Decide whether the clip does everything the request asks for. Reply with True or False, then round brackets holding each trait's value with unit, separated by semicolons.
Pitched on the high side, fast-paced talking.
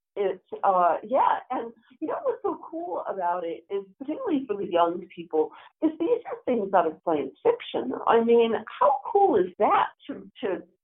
False (235 Hz; 185 wpm)